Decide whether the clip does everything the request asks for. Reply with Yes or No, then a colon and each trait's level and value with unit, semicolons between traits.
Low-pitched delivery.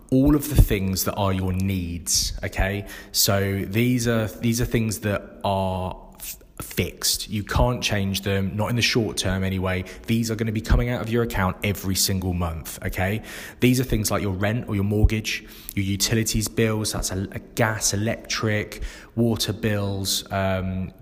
Yes: low, 105 Hz